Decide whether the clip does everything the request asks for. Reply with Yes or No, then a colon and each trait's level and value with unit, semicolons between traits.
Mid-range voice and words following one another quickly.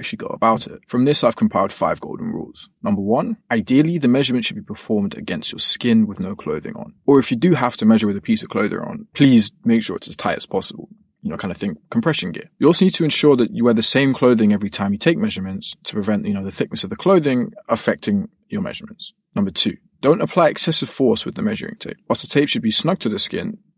Yes: medium, 180 Hz; fast, 255 wpm